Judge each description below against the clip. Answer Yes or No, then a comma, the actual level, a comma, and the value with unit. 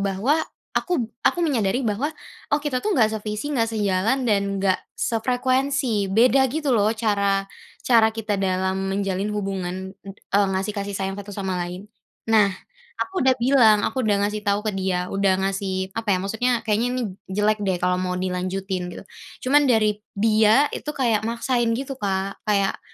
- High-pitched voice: Yes, high, 210 Hz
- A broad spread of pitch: No, average, 3.6 semitones